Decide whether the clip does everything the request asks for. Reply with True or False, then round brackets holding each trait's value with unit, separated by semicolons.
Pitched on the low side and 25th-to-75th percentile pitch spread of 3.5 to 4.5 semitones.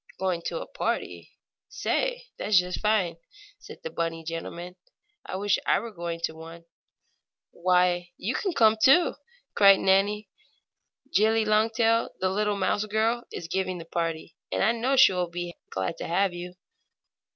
False (190 Hz; 4.1 semitones)